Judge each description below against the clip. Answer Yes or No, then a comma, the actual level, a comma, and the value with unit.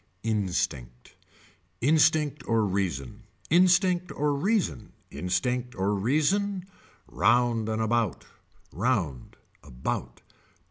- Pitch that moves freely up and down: Yes, wide, 8.4 semitones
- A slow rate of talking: Yes, slow, 85 wpm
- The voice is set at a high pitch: No, low, 120 Hz